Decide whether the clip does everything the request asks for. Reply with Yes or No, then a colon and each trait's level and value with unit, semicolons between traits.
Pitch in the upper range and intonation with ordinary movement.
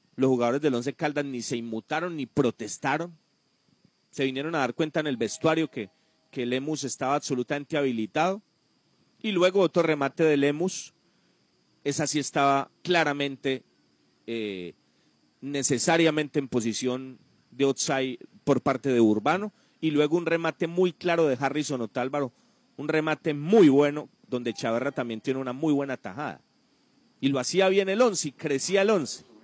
No: medium, 145 Hz; average, 4.0 semitones